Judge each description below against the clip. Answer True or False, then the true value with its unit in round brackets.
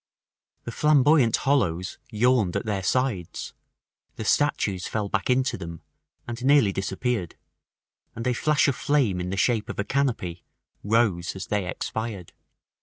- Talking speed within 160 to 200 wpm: False (145 wpm)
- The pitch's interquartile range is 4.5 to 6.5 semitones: True (5.2 semitones)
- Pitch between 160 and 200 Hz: False (110 Hz)